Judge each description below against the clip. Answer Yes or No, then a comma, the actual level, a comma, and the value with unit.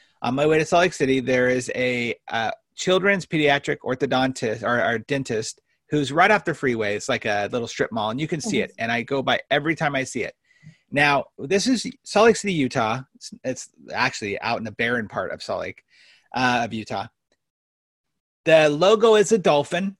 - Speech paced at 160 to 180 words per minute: No, fast, 205 wpm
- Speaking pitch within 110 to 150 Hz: Yes, medium, 140 Hz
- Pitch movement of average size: No, wide, 6.3 semitones